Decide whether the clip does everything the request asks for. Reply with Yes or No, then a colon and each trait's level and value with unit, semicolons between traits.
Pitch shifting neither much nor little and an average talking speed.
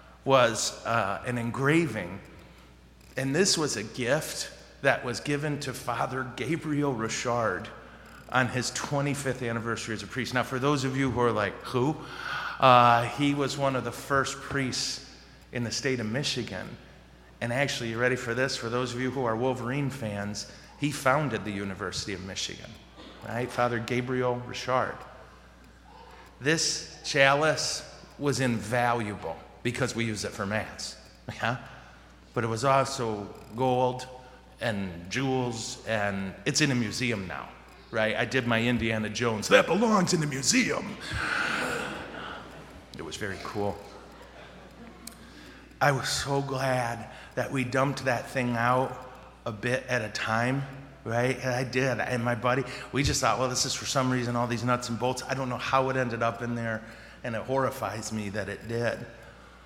Yes: average, 3.0 semitones; average, 160 wpm